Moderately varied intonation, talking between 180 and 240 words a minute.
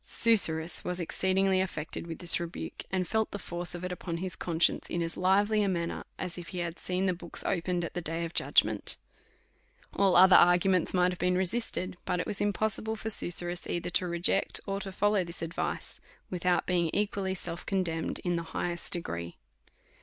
No: narrow, 1.9 semitones; average, 190 wpm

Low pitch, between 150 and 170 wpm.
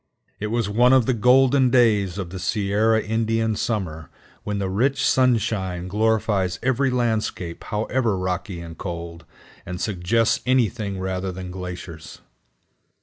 No: low, 105 Hz; slow, 135 wpm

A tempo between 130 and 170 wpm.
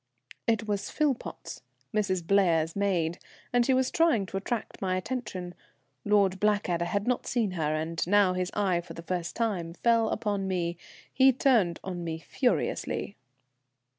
Yes: average, 155 wpm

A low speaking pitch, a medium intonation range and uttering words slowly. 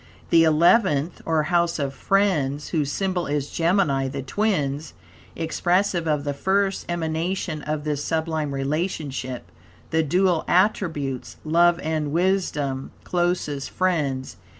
No: medium, 160 Hz; average, 3.6 semitones; slow, 120 wpm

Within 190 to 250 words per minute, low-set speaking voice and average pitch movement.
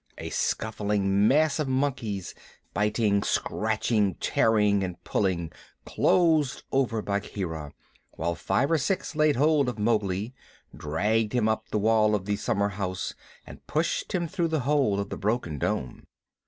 No: average, 140 wpm; low, 105 Hz; average, 4.8 semitones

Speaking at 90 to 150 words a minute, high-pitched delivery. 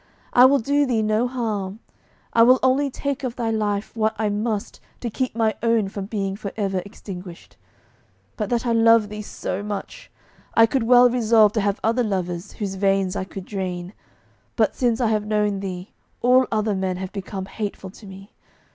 No: average, 190 wpm; high, 215 Hz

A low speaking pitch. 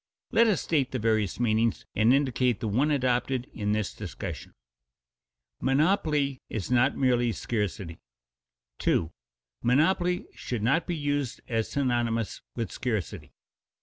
Yes: low, 125 Hz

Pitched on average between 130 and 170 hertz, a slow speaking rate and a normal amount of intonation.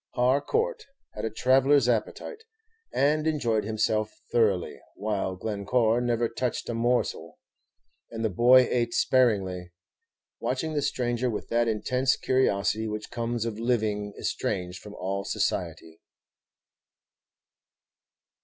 No: low, 115 Hz; slow, 115 wpm; average, 3.3 semitones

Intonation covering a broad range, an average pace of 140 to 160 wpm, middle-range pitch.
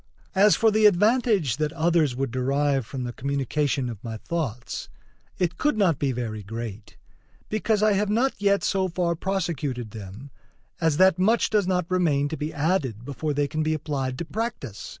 No: wide, 6.5 semitones; average, 180 wpm; medium, 155 Hz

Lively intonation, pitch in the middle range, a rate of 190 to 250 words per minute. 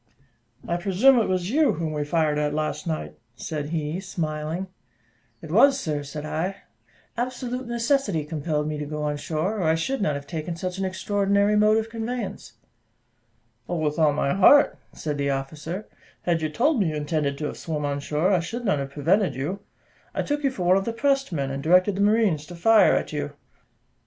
Yes: wide, 5.7 semitones; medium, 170 Hz; average, 200 wpm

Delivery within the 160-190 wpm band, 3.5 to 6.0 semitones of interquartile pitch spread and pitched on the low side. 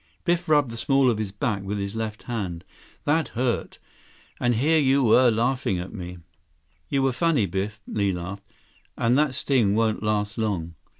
Yes: average, 175 wpm; average, 4.9 semitones; low, 115 Hz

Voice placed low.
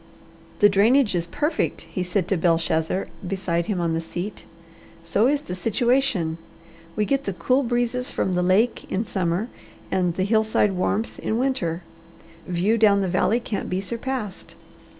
No: high, 195 Hz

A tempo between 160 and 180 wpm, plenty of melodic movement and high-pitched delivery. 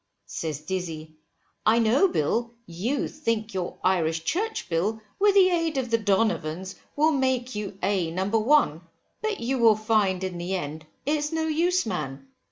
Yes: average, 165 wpm; wide, 8.0 semitones; high, 215 Hz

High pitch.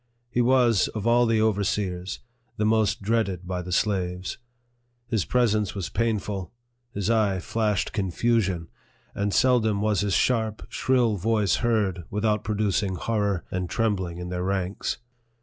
No: low, 105 Hz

